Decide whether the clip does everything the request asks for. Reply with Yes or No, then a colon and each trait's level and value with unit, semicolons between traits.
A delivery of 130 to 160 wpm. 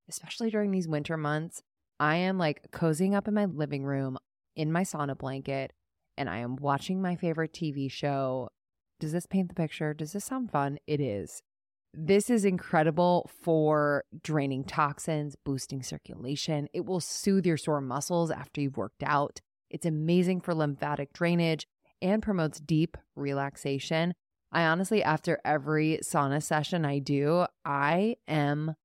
Yes: average, 155 wpm